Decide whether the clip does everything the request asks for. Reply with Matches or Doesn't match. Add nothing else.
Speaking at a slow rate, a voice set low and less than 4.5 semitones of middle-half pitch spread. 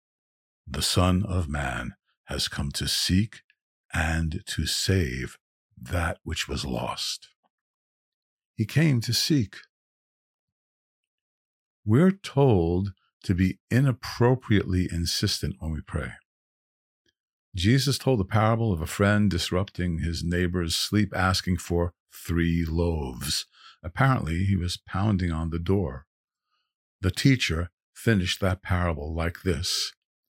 Matches